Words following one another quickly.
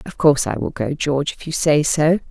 Yes: fast, 260 wpm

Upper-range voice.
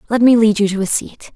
Yes: high, 215 Hz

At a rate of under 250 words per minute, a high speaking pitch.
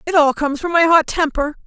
No: fast, 255 wpm; very high, 310 Hz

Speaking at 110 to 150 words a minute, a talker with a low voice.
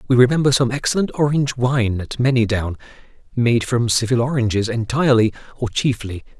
Yes: average, 140 wpm; low, 120 Hz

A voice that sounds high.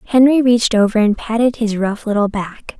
Yes: high, 225 Hz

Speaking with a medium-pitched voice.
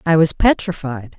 Yes: medium, 160 Hz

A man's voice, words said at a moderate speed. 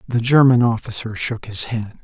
Yes: male; average, 175 wpm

